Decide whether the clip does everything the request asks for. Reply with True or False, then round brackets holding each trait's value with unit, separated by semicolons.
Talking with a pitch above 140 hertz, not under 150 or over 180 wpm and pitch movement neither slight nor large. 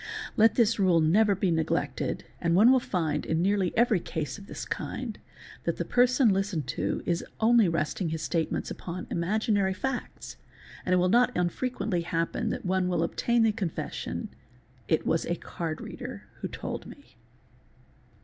True (185 Hz; 165 wpm; 4.7 semitones)